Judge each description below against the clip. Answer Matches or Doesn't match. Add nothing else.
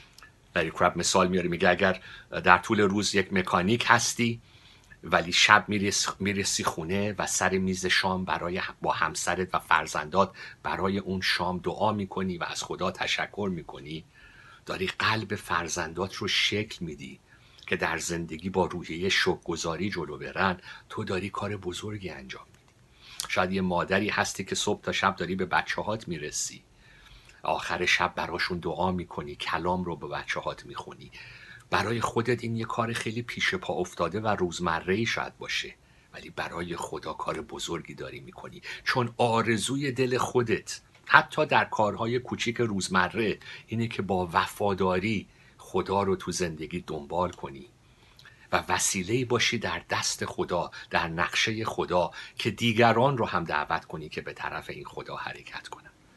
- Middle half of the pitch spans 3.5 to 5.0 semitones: Matches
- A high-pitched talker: Doesn't match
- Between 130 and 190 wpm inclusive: Matches